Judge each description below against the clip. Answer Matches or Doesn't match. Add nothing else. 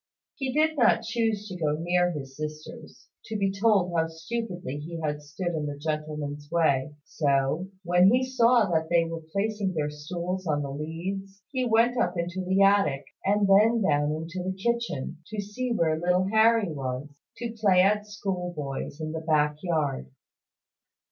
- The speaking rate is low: Doesn't match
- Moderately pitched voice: Matches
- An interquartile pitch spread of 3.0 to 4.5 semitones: Doesn't match